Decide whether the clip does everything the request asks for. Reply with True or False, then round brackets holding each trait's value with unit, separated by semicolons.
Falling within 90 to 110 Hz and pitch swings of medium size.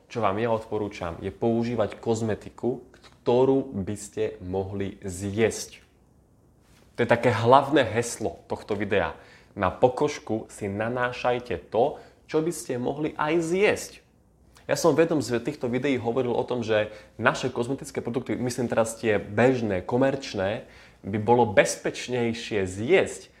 False (120 Hz; 3.3 semitones)